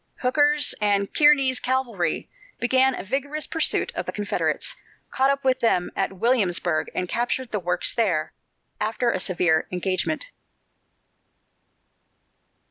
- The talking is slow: Yes, slow, 125 wpm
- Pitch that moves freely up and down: Yes, wide, 6.1 semitones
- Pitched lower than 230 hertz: No, high, 235 Hz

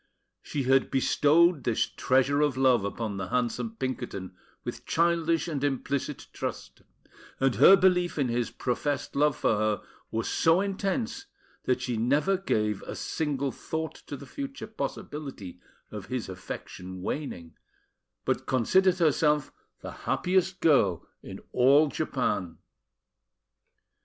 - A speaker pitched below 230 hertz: Yes, medium, 140 Hz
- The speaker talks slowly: Yes, slow, 130 wpm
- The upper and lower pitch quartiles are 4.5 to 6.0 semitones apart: Yes, wide, 5.5 semitones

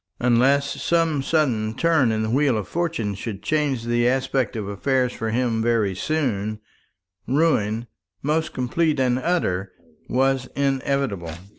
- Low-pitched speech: Yes, low, 125 Hz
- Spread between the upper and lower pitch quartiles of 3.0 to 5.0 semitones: Yes, average, 4.3 semitones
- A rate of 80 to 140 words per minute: Yes, slow, 135 wpm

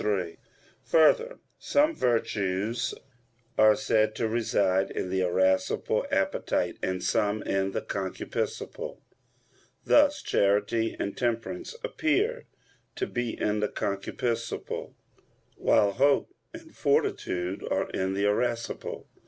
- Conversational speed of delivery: No, slow, 110 wpm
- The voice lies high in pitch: No, low, 110 Hz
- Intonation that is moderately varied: Yes, average, 4.5 semitones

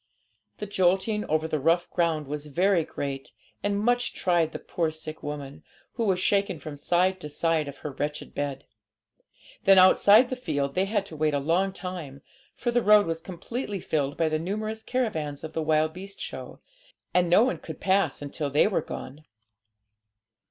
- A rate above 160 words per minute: Yes, average, 180 wpm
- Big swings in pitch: No, average, 4.7 semitones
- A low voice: No, medium, 165 Hz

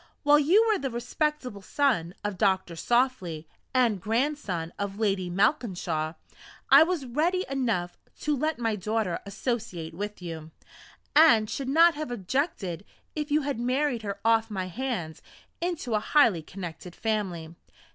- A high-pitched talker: Yes, high, 225 Hz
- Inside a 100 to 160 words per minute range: Yes, average, 145 wpm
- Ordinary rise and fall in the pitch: No, wide, 7.3 semitones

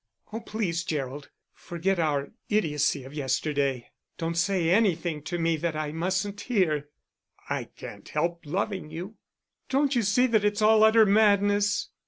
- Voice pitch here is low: No, medium, 175 Hz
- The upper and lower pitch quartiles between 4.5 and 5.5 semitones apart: Yes, average, 5.0 semitones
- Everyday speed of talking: Yes, average, 150 wpm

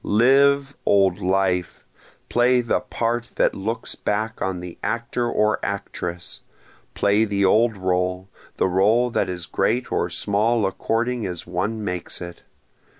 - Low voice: Yes, low, 105 Hz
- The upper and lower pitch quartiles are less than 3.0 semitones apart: No, average, 4.3 semitones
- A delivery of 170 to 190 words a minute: No, average, 140 wpm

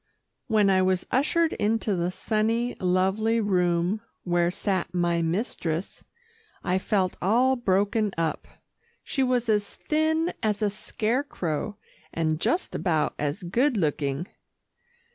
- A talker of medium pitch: No, high, 200 Hz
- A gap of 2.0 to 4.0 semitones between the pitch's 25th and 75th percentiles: No, average, 4.6 semitones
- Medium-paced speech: No, slow, 125 wpm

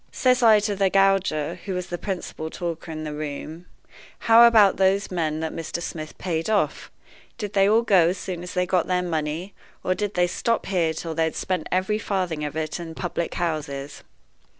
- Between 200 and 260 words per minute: Yes, fast, 205 wpm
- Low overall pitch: No, medium, 180 Hz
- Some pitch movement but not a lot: Yes, average, 3.4 semitones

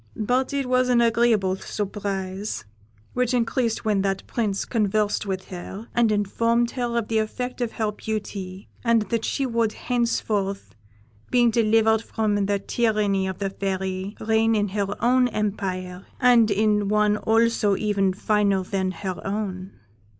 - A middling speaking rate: Yes, average, 150 wpm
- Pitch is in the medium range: No, high, 210 Hz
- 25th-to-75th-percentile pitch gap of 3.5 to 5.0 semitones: No, average, 2.9 semitones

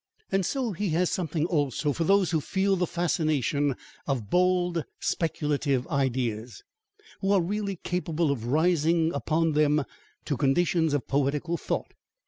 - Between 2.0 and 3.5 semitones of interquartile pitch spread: No, average, 3.9 semitones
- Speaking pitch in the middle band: Yes, medium, 160 Hz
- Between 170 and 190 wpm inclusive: No, average, 140 wpm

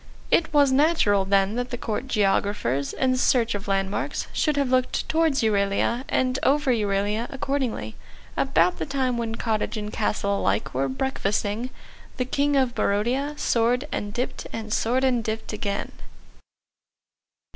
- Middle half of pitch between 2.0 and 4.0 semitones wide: No, average, 4.4 semitones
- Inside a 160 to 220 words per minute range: No, average, 145 wpm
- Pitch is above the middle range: Yes, high, 230 Hz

